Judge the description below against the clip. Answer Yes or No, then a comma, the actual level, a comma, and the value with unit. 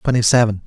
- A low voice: Yes, low, 115 Hz